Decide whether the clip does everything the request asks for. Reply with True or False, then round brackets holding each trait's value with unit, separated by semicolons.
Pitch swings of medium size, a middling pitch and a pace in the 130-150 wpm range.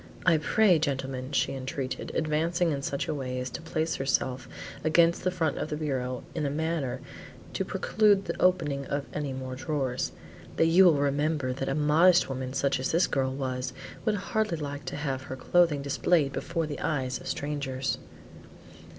False (3.6 semitones; 145 Hz; 180 wpm)